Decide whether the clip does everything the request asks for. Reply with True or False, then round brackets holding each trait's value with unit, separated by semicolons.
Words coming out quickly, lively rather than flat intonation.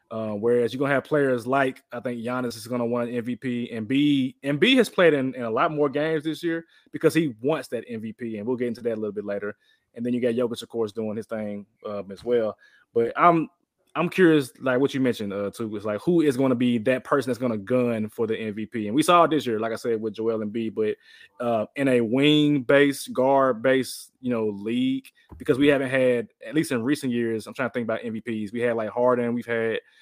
False (250 wpm; 3.4 semitones)